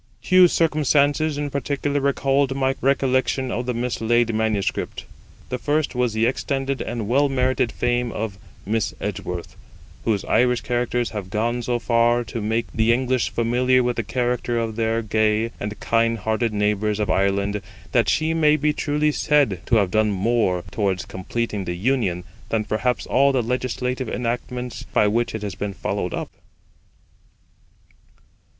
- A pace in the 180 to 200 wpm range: No, average, 155 wpm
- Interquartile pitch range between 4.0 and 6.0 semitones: No, average, 3.3 semitones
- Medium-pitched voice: No, low, 120 Hz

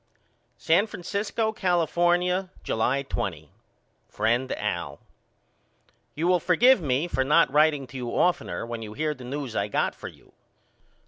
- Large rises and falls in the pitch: Yes, wide, 6.2 semitones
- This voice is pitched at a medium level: Yes, medium, 150 Hz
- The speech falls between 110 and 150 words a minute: Yes, average, 140 wpm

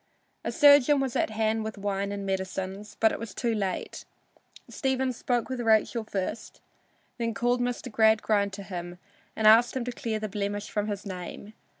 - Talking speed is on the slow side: No, average, 180 wpm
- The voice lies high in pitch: Yes, high, 215 Hz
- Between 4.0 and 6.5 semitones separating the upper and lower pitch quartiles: No, average, 3.0 semitones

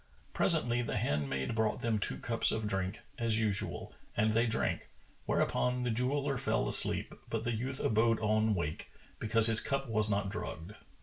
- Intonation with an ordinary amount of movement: No, narrow, 1.9 semitones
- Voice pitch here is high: No, low, 110 Hz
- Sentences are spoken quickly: No, average, 170 wpm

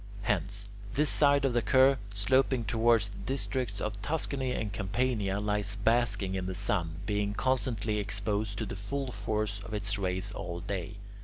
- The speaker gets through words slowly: No, average, 165 wpm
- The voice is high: No, low, 105 Hz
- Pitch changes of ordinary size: Yes, average, 3.4 semitones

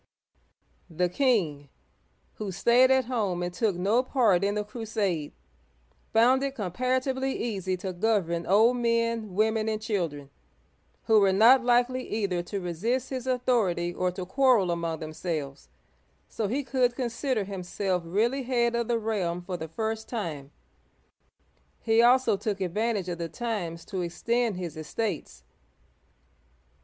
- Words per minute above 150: No, average, 140 wpm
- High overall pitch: Yes, high, 210 Hz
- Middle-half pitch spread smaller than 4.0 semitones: No, average, 5.1 semitones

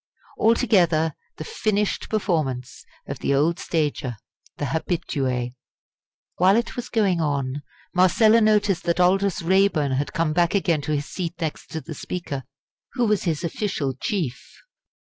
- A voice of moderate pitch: Yes, medium, 170 Hz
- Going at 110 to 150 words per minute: Yes, average, 145 wpm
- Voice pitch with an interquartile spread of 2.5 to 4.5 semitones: No, average, 5.1 semitones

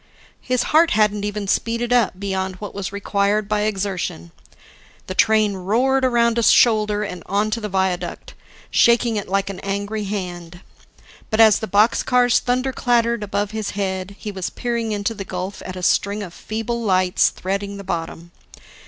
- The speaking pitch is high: Yes, high, 205 Hz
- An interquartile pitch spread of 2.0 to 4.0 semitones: Yes, average, 2.9 semitones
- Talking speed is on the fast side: No, average, 165 wpm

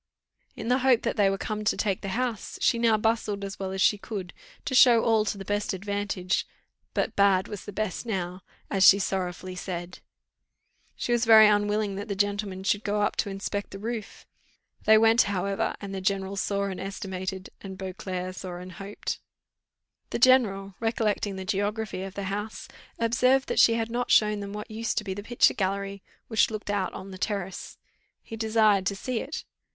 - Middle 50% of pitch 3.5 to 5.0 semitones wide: No, narrow, 2.4 semitones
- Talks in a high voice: Yes, high, 205 Hz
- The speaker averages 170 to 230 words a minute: Yes, average, 195 wpm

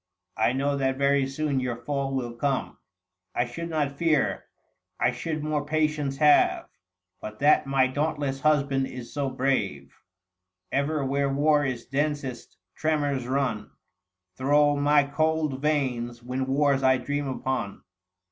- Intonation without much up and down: Yes, narrow, 2.1 semitones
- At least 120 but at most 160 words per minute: Yes, average, 140 wpm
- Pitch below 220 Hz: Yes, medium, 140 Hz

